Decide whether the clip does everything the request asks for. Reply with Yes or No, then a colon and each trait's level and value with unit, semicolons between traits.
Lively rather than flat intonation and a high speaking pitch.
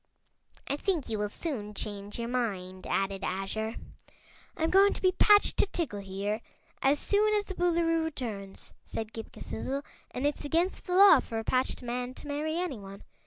Yes: wide, 8.1 semitones; very high, 255 Hz